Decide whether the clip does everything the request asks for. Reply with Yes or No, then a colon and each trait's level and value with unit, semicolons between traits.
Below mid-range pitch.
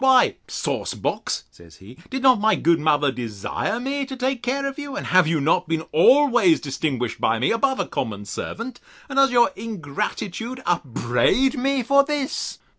No: high, 225 Hz